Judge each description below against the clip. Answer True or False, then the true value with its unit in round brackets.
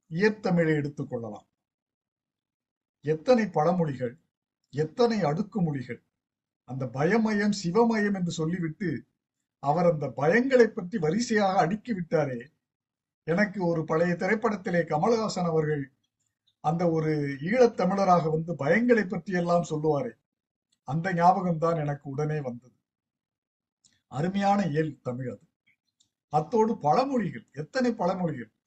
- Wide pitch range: True (6.0 semitones)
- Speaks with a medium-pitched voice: True (165 Hz)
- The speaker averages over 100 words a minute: False (95 wpm)